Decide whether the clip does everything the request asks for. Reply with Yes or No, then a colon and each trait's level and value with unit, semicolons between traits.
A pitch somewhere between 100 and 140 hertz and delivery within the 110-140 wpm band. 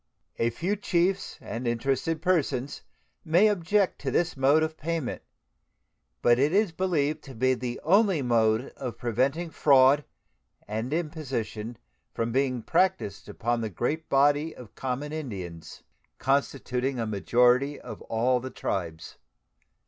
Yes: low, 135 Hz; slow, 135 wpm